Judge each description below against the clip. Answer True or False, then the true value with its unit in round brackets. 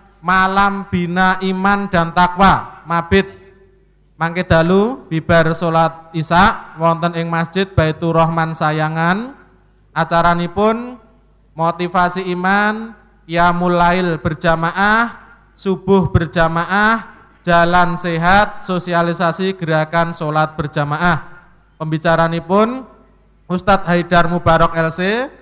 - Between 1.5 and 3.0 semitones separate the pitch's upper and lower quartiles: True (2.7 semitones)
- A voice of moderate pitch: True (175 Hz)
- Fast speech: False (90 wpm)